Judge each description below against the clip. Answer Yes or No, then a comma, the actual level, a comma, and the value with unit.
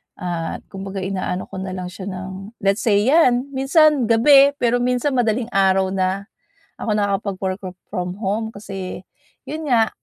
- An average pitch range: Yes, average, 4.4 semitones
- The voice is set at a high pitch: Yes, high, 200 Hz